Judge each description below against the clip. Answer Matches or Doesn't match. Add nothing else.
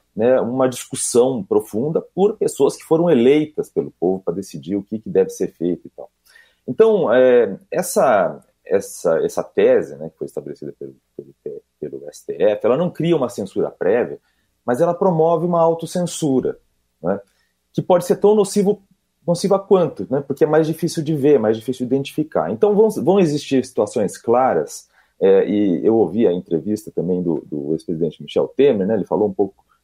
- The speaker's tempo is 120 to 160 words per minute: Doesn't match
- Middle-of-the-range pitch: Matches